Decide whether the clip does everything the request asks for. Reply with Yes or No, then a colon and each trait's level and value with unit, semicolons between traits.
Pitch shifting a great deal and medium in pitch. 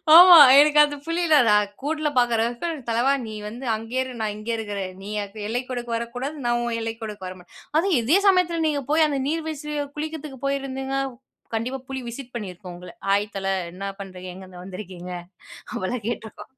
No: wide, 5.9 semitones; high, 240 Hz